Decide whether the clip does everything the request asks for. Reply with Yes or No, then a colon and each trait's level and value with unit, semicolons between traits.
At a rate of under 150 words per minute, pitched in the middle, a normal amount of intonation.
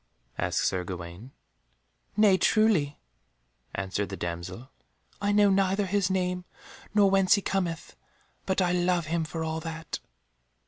No: slow, 135 wpm; medium, 175 Hz; wide, 6.5 semitones